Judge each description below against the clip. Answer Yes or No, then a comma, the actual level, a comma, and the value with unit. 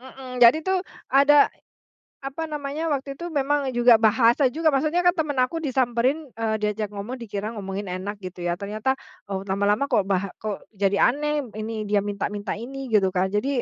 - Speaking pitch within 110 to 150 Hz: No, high, 235 Hz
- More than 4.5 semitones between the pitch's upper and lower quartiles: Yes, average, 5.3 semitones